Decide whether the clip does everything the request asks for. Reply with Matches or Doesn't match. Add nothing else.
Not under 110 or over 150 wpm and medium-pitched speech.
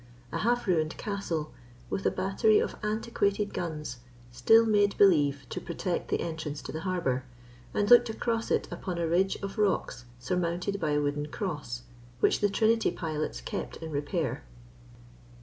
Doesn't match